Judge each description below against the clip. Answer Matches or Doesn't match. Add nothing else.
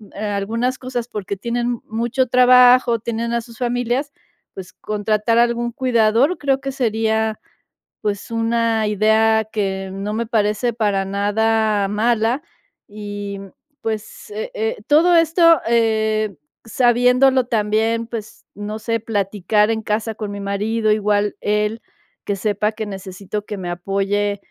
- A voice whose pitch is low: Doesn't match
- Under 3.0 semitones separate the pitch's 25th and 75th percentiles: Matches